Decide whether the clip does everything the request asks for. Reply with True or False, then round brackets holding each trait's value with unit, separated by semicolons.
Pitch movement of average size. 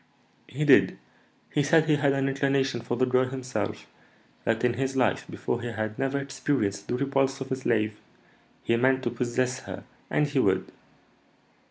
False (2.3 semitones)